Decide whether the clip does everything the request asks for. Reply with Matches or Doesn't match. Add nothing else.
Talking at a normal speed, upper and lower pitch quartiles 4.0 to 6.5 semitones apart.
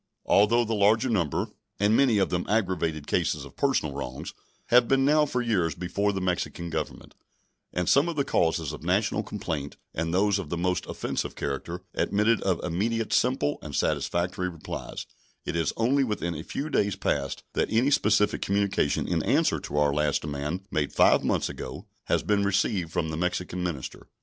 Matches